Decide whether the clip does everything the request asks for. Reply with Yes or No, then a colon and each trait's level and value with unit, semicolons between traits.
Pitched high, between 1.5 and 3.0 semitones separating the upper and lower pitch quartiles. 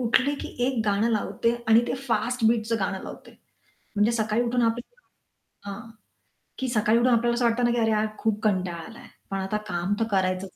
Yes: high, 225 Hz; narrow, 2.6 semitones